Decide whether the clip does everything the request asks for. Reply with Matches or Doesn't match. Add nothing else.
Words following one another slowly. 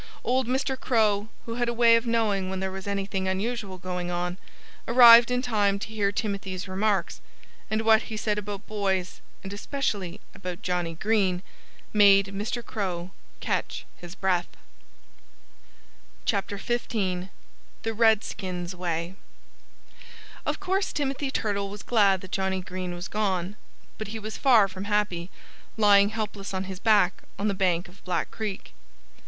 Doesn't match